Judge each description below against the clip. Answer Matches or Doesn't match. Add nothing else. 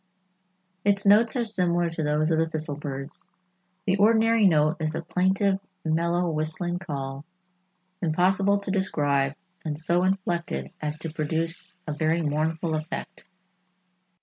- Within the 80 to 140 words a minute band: Matches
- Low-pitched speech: Doesn't match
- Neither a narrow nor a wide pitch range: Matches